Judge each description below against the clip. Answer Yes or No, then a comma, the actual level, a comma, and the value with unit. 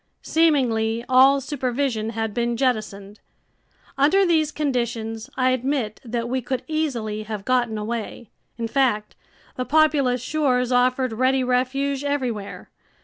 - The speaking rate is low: Yes, slow, 125 wpm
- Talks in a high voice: Yes, very high, 250 Hz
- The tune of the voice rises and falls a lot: No, average, 3.4 semitones